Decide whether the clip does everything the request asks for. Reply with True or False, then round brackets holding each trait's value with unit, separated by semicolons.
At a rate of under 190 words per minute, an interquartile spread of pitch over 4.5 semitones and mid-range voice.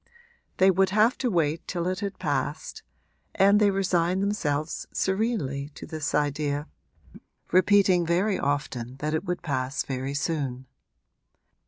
True (135 wpm; 5.1 semitones; 170 Hz)